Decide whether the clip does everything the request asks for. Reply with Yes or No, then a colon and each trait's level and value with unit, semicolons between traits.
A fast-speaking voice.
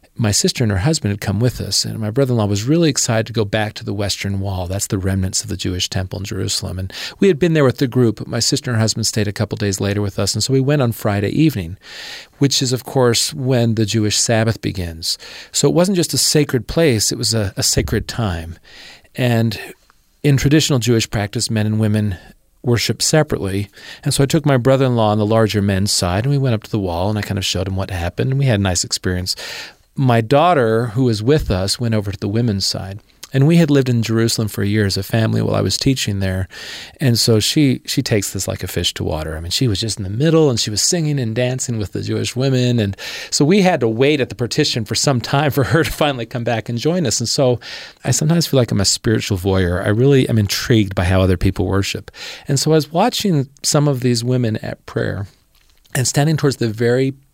Yes: fast, 255 wpm